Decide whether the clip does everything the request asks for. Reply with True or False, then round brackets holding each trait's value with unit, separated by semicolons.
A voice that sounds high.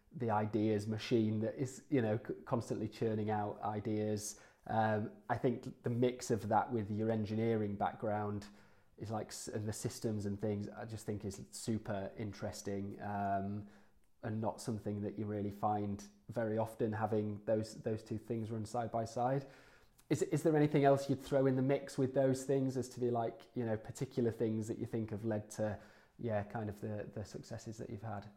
False (110 Hz)